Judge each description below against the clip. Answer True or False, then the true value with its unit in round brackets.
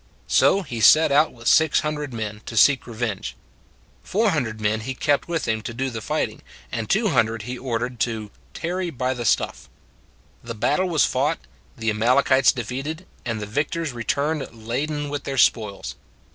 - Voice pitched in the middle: False (125 Hz)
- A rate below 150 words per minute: False (180 wpm)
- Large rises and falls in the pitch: False (4.8 semitones)